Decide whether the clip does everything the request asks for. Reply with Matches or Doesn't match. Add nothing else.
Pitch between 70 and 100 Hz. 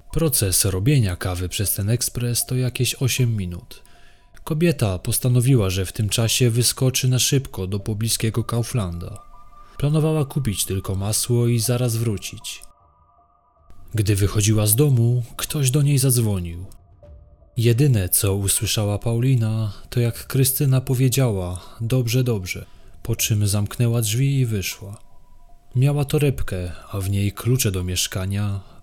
Doesn't match